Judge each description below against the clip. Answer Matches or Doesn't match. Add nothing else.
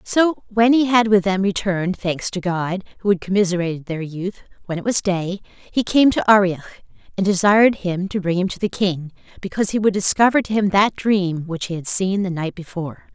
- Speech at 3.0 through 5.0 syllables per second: Doesn't match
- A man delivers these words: Doesn't match